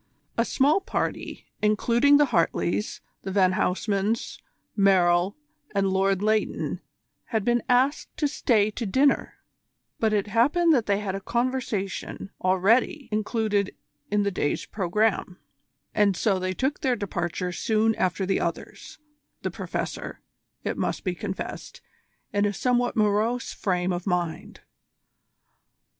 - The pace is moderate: No, slow, 130 wpm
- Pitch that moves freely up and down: No, average, 3.8 semitones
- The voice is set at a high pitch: Yes, high, 210 Hz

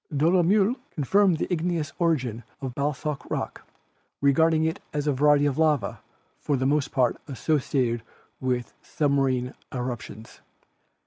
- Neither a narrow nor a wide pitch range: Yes, average, 3.7 semitones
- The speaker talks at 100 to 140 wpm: Yes, slow, 135 wpm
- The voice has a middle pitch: Yes, medium, 145 Hz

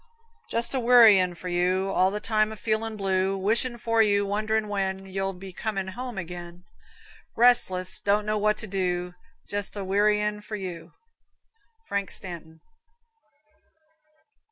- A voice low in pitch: No, high, 200 Hz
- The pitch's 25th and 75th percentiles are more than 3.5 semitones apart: No, narrow, 2.4 semitones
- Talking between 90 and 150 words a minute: Yes, average, 140 wpm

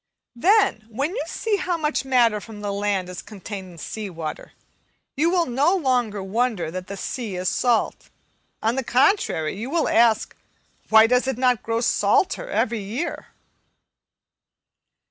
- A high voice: Yes, high, 230 Hz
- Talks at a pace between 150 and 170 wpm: Yes, average, 155 wpm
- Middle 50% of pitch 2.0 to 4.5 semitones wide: No, average, 5.1 semitones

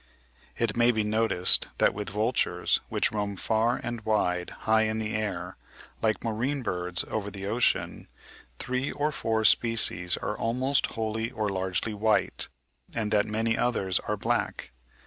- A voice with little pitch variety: Yes, narrow, 2.0 semitones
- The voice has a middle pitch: No, low, 110 Hz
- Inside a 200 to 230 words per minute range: No, average, 155 wpm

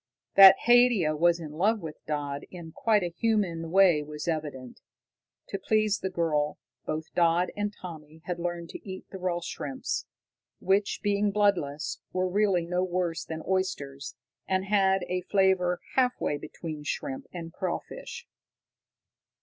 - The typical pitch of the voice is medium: Yes, medium, 180 Hz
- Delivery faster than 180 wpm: No, average, 150 wpm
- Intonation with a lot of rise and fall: No, average, 3.5 semitones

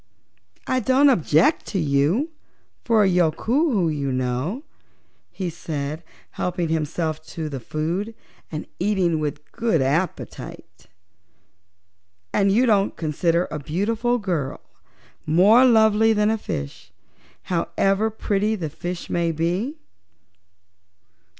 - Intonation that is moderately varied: No, wide, 5.8 semitones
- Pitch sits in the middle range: Yes, medium, 180 Hz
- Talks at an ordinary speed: No, slow, 110 wpm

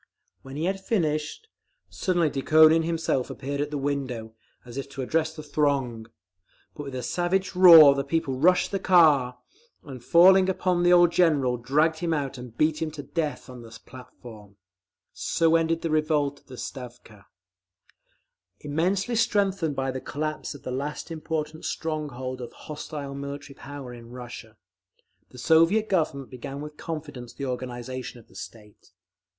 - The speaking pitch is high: No, medium, 145 Hz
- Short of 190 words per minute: Yes, average, 160 wpm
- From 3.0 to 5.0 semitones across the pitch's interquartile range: Yes, average, 4.1 semitones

